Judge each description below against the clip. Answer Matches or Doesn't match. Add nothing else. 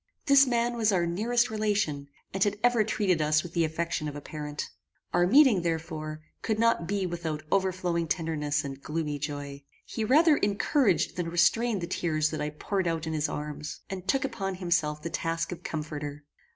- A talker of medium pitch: Matches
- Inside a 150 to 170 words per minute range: Doesn't match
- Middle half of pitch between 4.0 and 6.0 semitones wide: Matches